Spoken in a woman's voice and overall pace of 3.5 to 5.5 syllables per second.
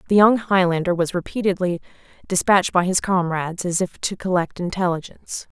No: female; 5.8 syllables/s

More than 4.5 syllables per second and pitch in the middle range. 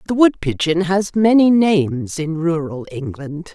No: 4.2 syllables/s; medium, 170 Hz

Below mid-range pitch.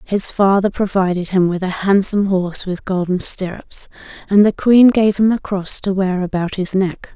No: high, 190 Hz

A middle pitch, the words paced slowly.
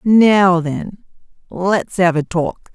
Yes: medium, 180 Hz; slow, 130 wpm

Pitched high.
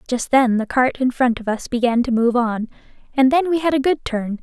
Yes: very high, 250 Hz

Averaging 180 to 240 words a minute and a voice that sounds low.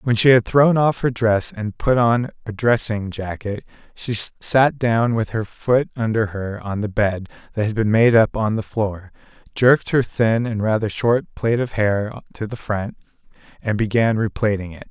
Yes: average, 195 wpm; low, 110 Hz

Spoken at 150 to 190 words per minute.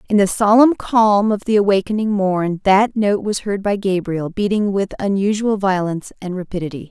Yes: average, 175 wpm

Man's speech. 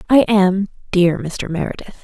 No: female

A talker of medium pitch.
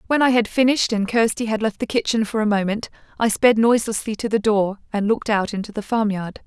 No: high, 215 Hz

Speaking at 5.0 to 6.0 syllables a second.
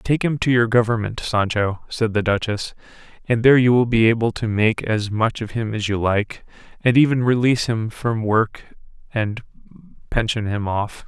No: 4.8 syllables/s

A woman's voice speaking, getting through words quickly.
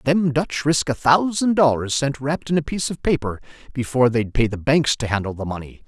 No: male; fast, 225 wpm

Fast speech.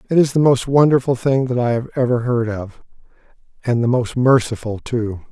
No: average, 190 wpm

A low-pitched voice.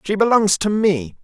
No: high, 195 Hz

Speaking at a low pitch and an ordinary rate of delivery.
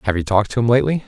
No: low, 115 Hz; fast, 335 wpm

